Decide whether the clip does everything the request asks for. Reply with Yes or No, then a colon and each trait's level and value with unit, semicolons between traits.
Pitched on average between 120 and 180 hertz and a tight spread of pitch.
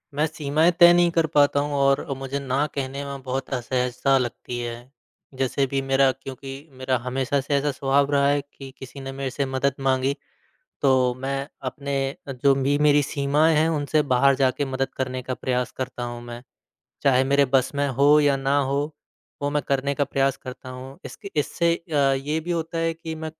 Yes: medium, 140 Hz; narrow, 1.5 semitones